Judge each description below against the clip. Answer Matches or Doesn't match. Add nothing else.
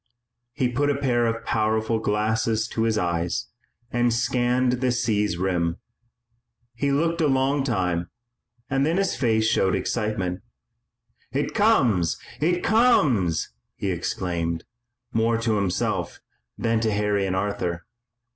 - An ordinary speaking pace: Doesn't match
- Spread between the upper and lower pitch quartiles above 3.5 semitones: Matches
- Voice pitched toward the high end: Doesn't match